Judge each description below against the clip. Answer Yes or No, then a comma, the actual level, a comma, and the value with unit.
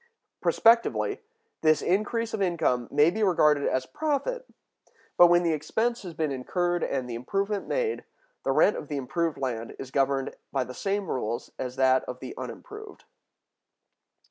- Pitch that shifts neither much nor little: No, wide, 8.0 semitones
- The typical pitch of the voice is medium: Yes, medium, 165 Hz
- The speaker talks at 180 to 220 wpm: No, average, 160 wpm